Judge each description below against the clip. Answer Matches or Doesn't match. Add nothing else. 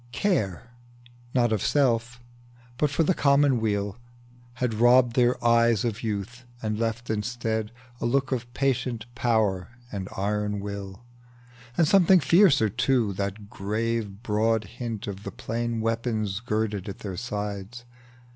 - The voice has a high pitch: Doesn't match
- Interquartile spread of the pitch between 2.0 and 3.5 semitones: Matches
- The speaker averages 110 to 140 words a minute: Matches